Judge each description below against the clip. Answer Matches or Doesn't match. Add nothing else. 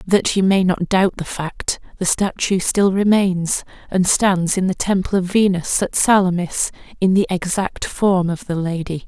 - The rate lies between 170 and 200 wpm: Matches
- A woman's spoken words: Matches